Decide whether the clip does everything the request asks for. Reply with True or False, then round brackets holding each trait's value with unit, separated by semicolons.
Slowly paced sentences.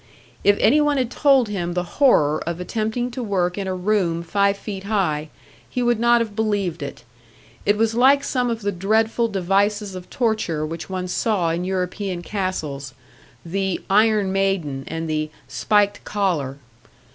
False (165 wpm)